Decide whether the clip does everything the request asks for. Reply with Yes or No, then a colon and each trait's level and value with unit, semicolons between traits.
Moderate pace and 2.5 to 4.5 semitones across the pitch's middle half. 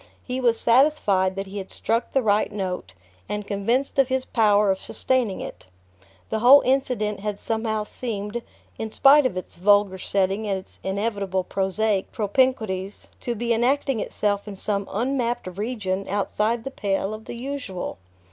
Yes: average, 160 wpm; average, 3.5 semitones